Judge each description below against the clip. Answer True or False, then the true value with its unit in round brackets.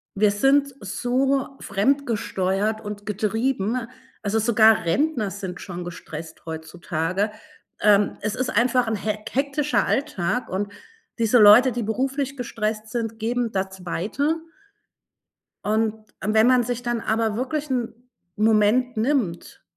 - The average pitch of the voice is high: True (220 Hz)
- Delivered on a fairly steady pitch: False (3.5 semitones)